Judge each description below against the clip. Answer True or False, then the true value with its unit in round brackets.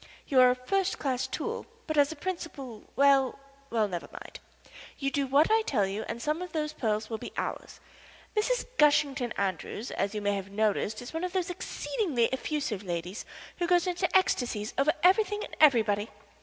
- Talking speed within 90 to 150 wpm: False (185 wpm)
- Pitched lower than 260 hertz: False (275 Hz)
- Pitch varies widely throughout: True (7.7 semitones)